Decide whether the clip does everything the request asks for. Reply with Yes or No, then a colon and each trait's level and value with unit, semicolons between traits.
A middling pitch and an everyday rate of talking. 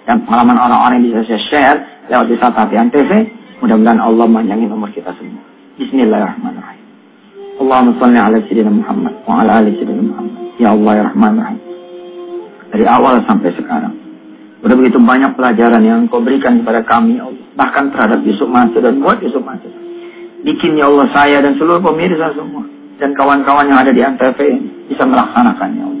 Yes: medium, 175 Hz; average, 170 wpm